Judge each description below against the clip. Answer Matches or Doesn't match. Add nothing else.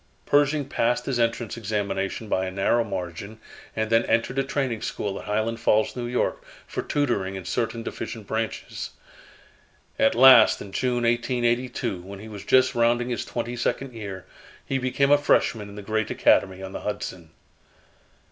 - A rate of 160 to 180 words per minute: Matches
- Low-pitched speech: Matches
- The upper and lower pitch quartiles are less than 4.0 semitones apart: Matches